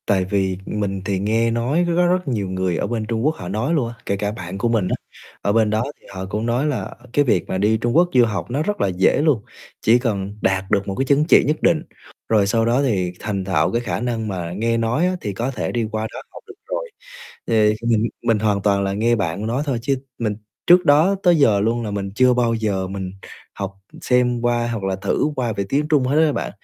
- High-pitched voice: No, low, 115 Hz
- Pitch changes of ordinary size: Yes, average, 4.4 semitones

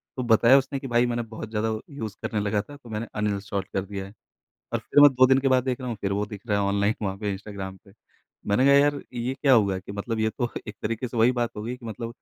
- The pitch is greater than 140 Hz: No, low, 110 Hz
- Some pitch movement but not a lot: Yes, average, 3.7 semitones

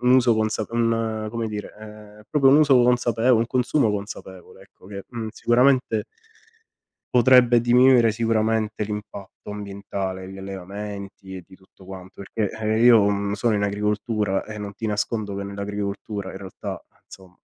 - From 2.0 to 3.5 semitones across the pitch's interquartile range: Yes, average, 2.7 semitones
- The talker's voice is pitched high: No, low, 105 Hz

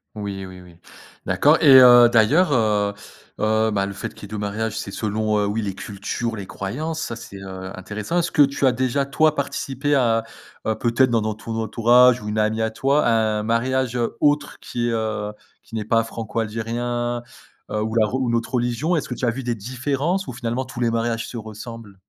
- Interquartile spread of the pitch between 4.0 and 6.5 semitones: No, average, 2.9 semitones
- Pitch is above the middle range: No, low, 115 Hz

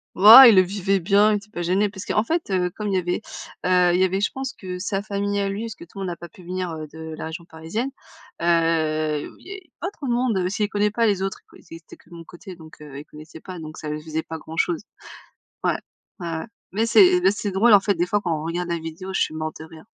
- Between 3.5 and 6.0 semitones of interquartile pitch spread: Yes, average, 3.9 semitones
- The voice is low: No, medium, 185 Hz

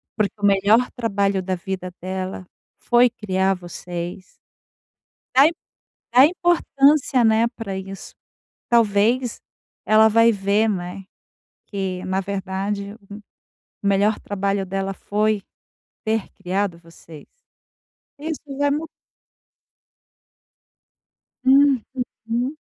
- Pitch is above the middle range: Yes, high, 200 Hz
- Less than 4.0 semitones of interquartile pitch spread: Yes, average, 3.5 semitones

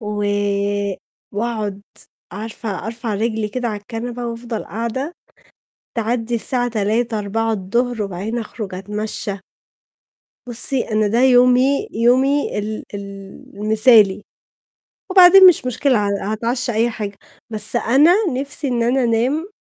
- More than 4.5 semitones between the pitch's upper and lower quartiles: No, average, 2.7 semitones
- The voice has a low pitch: No, high, 230 Hz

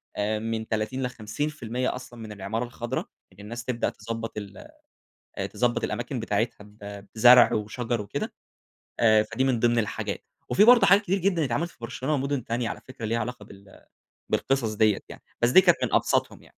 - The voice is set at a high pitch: No, low, 115 Hz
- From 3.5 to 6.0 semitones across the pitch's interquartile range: No, average, 3.1 semitones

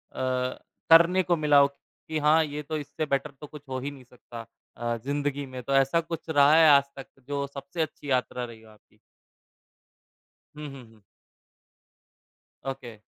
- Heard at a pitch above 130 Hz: Yes, medium, 140 Hz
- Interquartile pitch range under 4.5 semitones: Yes, average, 2.7 semitones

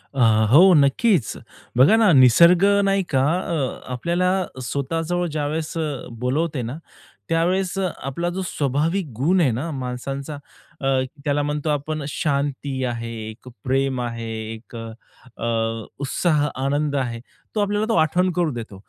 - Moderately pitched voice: Yes, medium, 145 Hz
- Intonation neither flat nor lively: Yes, average, 4.6 semitones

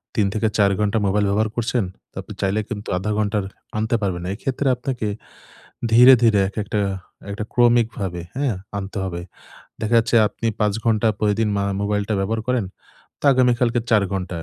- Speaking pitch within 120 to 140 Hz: No, low, 110 Hz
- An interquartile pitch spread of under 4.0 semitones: Yes, narrow, 2.6 semitones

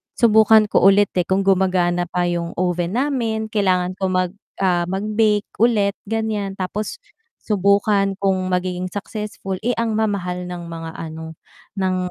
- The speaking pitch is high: Yes, high, 195 Hz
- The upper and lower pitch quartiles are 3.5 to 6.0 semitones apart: No, average, 2.9 semitones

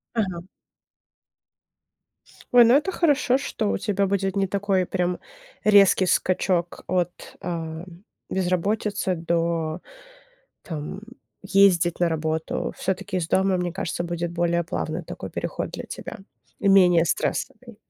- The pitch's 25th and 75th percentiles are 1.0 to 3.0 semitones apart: Yes, narrow, 2.6 semitones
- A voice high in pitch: No, medium, 180 Hz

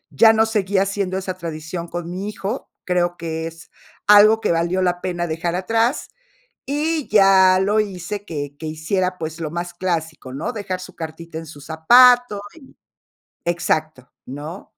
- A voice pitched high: No, medium, 180 Hz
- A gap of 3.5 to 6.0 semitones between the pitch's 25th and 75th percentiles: Yes, average, 3.8 semitones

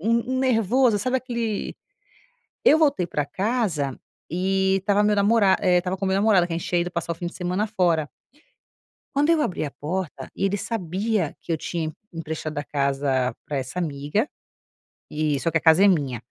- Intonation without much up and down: No, average, 4.9 semitones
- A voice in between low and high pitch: Yes, medium, 180 Hz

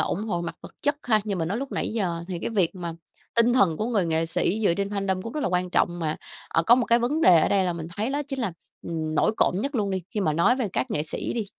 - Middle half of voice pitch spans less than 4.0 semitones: No, wide, 5.4 semitones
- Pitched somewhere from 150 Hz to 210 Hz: Yes, high, 195 Hz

